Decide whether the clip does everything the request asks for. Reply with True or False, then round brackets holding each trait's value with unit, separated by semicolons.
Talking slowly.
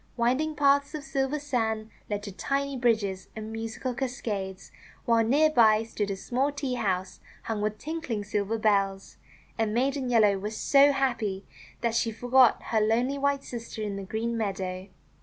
False (165 wpm)